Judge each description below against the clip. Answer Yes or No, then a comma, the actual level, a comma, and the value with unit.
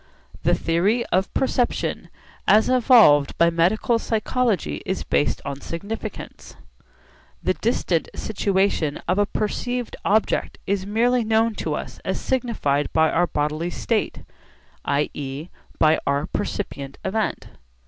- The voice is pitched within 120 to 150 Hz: No, high, 195 Hz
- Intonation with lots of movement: Yes, wide, 6.5 semitones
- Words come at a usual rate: No, slow, 120 wpm